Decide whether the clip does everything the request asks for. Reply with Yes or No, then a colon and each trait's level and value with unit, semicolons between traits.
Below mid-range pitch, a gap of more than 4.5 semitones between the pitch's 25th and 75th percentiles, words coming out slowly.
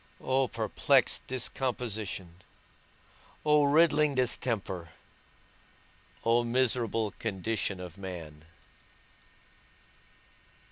Yes: low, 115 Hz; wide, 5.5 semitones; slow, 60 wpm